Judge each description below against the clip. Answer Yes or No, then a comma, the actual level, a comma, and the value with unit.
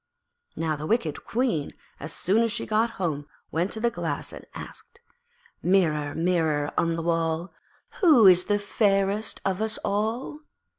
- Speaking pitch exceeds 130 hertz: Yes, high, 190 Hz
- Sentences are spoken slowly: No, average, 150 wpm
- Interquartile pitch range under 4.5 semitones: No, average, 5.0 semitones